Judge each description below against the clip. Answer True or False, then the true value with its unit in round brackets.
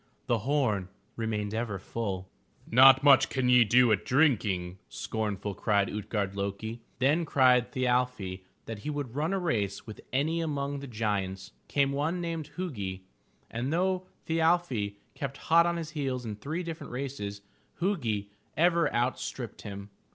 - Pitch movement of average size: False (6.2 semitones)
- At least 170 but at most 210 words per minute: False (155 wpm)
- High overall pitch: False (125 Hz)